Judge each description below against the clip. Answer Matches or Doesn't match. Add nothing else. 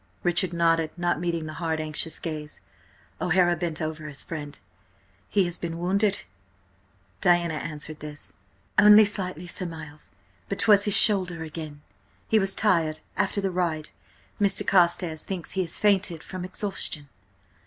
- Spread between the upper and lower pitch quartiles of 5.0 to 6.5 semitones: Doesn't match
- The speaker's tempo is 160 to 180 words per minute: Doesn't match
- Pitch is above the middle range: Doesn't match